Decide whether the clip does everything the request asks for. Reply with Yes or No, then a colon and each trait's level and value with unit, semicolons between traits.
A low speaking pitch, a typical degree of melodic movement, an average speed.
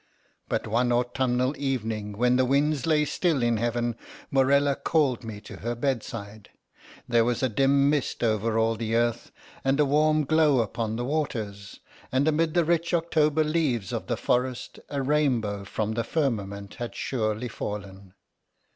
Yes: low, 125 Hz; average, 4.3 semitones; average, 160 wpm